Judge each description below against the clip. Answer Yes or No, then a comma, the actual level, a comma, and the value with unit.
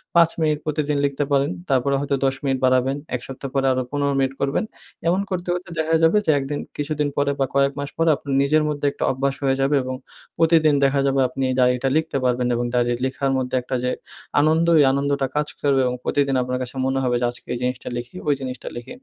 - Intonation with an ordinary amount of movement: No, narrow, 2.3 semitones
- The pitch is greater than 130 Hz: Yes, medium, 140 Hz